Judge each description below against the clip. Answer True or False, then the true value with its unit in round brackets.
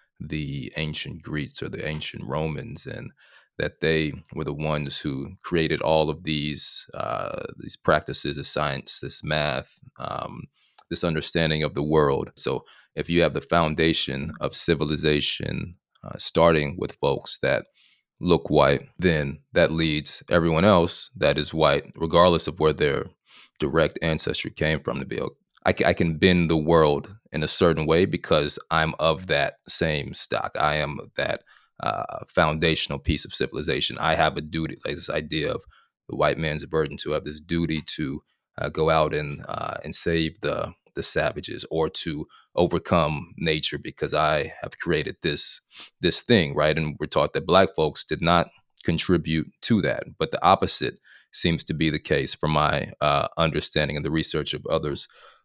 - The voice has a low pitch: True (80 Hz)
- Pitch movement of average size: False (1.2 semitones)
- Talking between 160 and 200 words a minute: True (170 wpm)